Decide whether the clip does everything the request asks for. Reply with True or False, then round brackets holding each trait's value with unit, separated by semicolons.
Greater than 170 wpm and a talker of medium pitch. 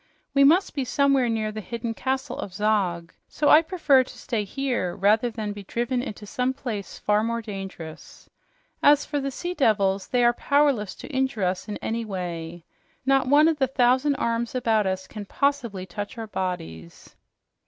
False (180 wpm; 230 Hz)